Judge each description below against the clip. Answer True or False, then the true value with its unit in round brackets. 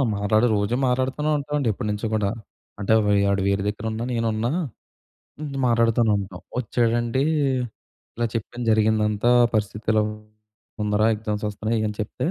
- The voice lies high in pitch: False (110 Hz)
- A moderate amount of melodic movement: False (2.2 semitones)